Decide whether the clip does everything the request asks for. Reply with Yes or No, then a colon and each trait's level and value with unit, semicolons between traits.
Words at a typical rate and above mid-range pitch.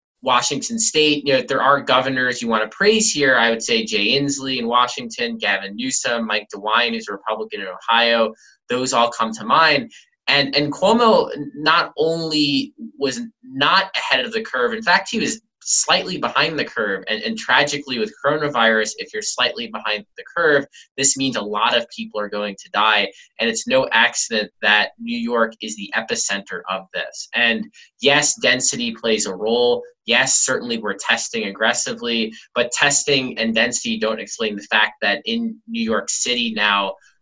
No: average, 175 wpm; low, 135 Hz